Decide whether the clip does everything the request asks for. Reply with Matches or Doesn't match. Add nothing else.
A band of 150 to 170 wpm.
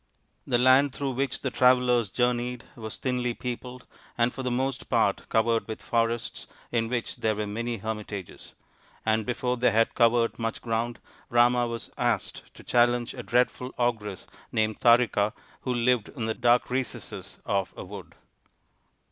Matches